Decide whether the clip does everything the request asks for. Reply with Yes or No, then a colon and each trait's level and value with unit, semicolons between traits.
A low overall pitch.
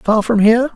No: high, 225 Hz